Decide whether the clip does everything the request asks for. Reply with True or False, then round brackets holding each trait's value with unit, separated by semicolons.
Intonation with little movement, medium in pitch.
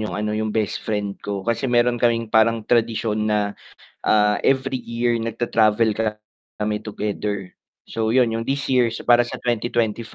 False (2.0 semitones; 115 Hz)